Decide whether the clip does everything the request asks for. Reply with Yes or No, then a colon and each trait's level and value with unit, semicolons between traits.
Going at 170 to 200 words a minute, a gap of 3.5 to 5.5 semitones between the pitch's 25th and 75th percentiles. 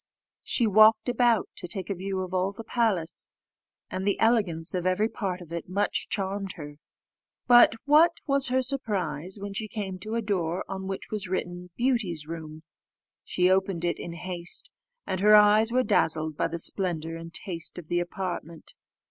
Yes: average, 180 wpm; average, 3.8 semitones